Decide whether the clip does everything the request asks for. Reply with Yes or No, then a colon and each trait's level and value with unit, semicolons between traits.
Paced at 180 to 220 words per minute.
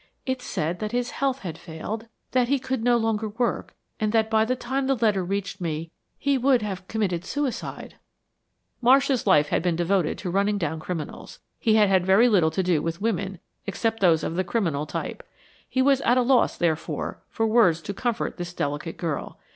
Yes: average, 195 wpm